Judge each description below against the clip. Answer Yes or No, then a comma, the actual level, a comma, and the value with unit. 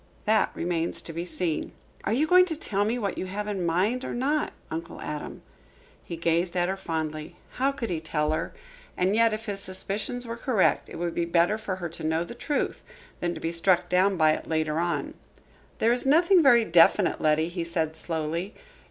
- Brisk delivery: Yes, fast, 215 wpm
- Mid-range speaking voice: Yes, medium, 180 Hz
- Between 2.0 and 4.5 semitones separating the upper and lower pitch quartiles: No, average, 5.1 semitones